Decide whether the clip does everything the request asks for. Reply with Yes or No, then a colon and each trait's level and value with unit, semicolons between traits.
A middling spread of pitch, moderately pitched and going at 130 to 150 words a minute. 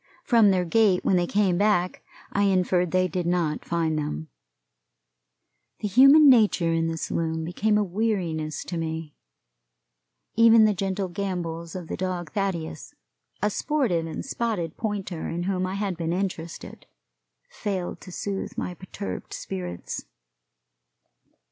Yes: average, 3.5 semitones; medium, 180 Hz; average, 140 wpm